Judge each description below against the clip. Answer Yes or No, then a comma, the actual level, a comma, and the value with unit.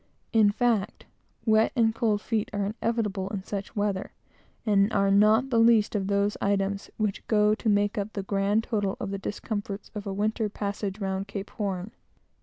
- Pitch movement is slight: Yes, narrow, 1.6 semitones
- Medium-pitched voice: No, high, 205 Hz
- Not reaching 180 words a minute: No, average, 185 wpm